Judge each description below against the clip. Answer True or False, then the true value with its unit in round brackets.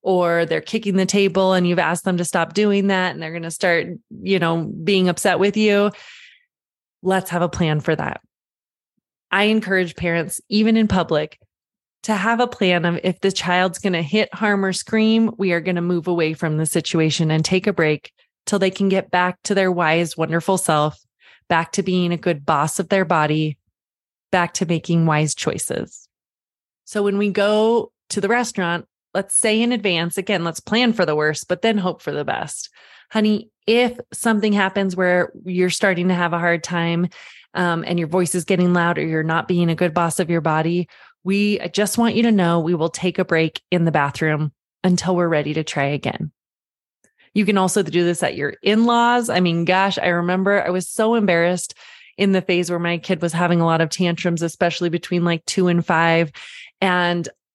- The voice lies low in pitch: False (180 Hz)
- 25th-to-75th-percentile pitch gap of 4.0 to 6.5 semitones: False (2.8 semitones)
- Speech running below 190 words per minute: False (200 wpm)